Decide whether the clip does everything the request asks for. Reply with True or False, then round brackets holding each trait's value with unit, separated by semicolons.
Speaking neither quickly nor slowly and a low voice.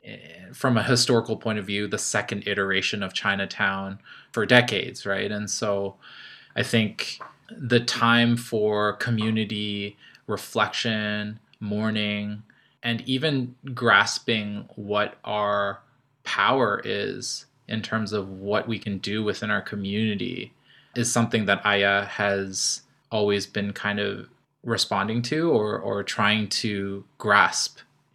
False (120 wpm; 105 Hz)